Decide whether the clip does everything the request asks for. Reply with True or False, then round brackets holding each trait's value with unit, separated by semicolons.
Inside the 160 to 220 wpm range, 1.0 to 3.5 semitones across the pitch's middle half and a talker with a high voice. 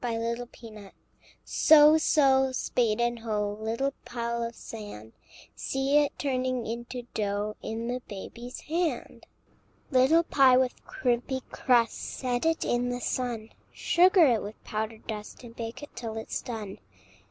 False (140 wpm; 2.9 semitones; 240 Hz)